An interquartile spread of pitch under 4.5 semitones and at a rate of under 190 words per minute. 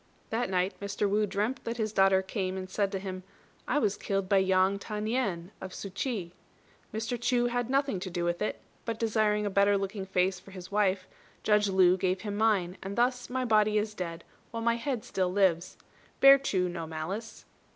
No: average, 3.0 semitones; fast, 205 wpm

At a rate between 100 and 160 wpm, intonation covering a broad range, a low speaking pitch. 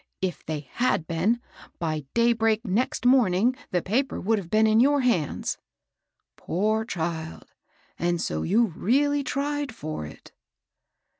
No: average, 140 wpm; wide, 6.4 semitones; high, 215 Hz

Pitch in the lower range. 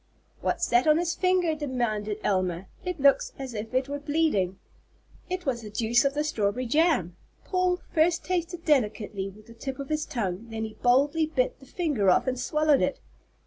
No: very high, 270 Hz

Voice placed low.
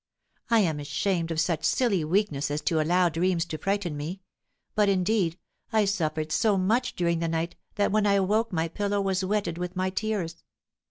No: medium, 185 Hz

